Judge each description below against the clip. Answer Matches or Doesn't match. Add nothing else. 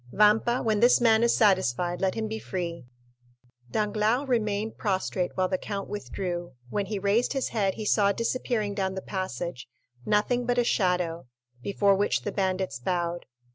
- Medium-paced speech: Matches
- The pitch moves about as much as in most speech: Matches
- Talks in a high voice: Matches